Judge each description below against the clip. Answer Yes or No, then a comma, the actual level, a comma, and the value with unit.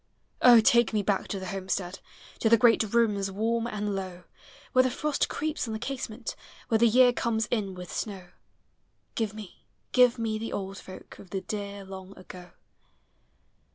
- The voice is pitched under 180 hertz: No, high, 215 Hz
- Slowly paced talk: No, average, 175 wpm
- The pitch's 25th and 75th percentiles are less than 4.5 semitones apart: Yes, average, 3.2 semitones